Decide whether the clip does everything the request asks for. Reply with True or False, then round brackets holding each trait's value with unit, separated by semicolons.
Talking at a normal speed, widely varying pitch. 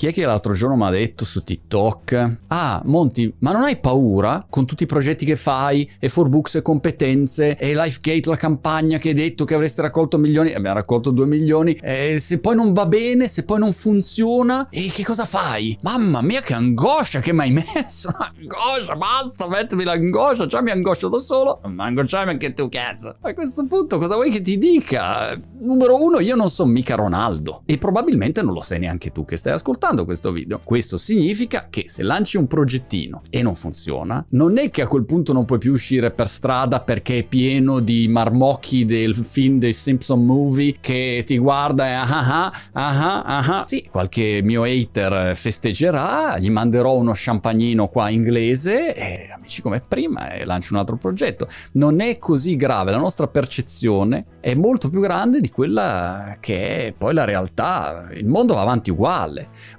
False (190 wpm; 6.6 semitones)